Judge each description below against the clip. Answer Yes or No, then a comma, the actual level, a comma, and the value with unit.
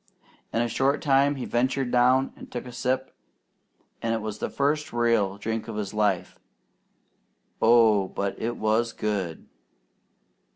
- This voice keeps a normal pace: Yes, average, 150 wpm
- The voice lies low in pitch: Yes, low, 115 Hz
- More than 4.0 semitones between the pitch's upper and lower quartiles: No, average, 3.3 semitones